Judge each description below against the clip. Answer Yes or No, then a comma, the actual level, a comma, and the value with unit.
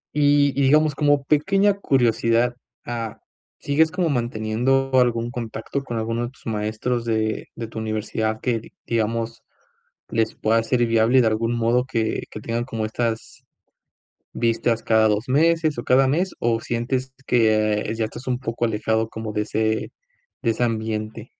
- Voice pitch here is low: Yes, low, 115 Hz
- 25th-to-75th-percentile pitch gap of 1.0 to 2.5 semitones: No, average, 2.9 semitones